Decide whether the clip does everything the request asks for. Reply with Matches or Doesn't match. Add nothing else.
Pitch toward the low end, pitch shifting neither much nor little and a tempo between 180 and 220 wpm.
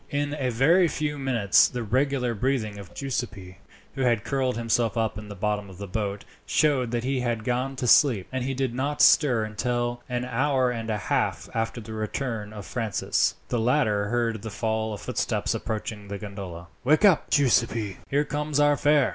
Matches